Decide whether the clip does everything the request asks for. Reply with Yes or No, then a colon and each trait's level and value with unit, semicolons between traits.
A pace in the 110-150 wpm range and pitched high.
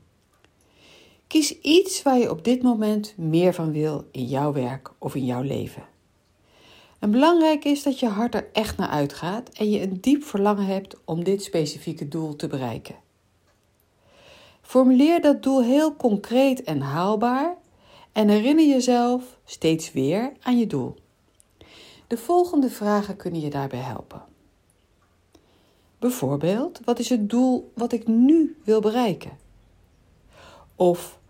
Yes: average, 140 wpm; high, 200 Hz